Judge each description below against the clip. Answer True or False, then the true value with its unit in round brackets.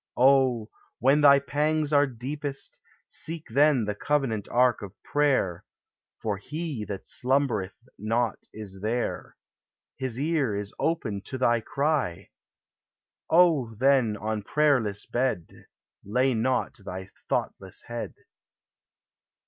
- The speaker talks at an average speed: False (115 wpm)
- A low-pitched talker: True (125 Hz)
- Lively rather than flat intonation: False (5.0 semitones)